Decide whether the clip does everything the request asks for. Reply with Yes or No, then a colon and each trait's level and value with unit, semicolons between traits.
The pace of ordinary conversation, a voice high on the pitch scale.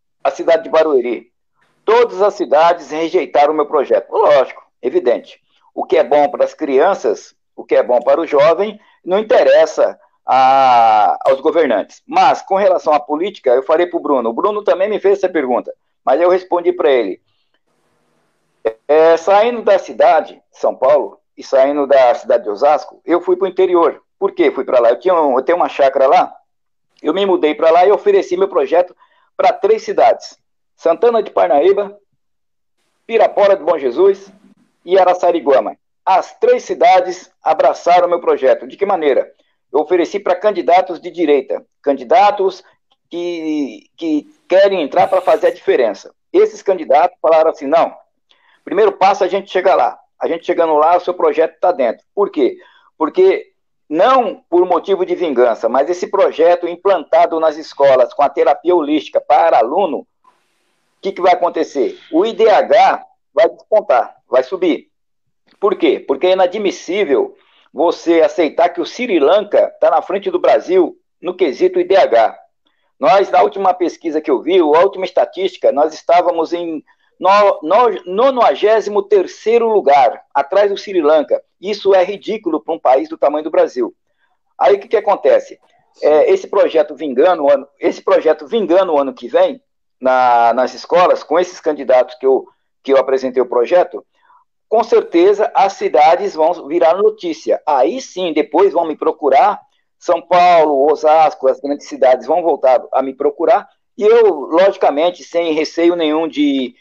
Yes: average, 165 wpm; high, 200 Hz